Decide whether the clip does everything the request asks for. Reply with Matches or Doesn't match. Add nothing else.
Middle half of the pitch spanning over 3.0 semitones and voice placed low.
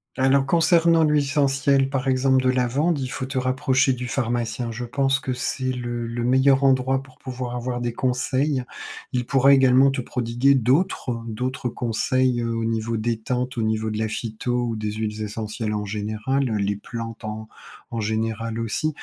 Doesn't match